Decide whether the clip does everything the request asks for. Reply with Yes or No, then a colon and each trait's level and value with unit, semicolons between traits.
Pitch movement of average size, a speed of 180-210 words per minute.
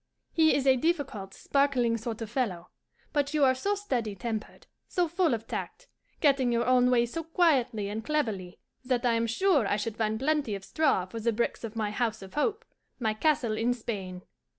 Yes: average, 4.8 semitones; average, 200 wpm